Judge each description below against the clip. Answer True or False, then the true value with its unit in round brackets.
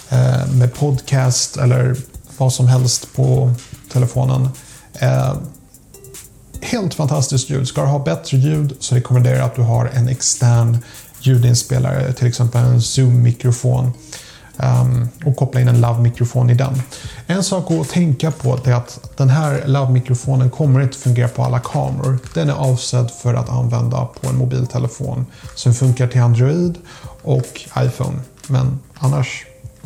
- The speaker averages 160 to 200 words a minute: False (145 wpm)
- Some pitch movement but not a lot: False (1.5 semitones)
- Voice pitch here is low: True (130 Hz)